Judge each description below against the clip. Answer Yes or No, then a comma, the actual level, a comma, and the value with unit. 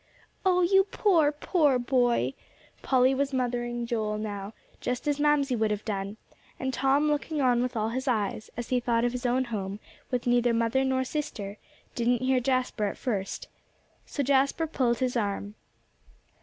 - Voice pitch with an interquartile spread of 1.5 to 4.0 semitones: Yes, average, 2.9 semitones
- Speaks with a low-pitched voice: No, very high, 250 Hz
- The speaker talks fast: No, average, 170 wpm